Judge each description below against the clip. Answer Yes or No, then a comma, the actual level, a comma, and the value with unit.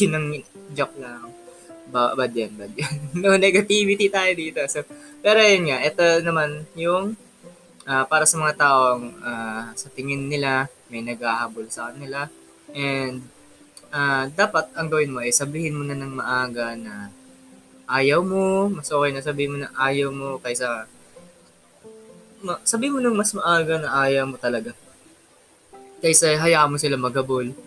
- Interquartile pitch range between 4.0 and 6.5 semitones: Yes, average, 5.2 semitones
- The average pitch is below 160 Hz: Yes, medium, 140 Hz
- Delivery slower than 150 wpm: No, fast, 155 wpm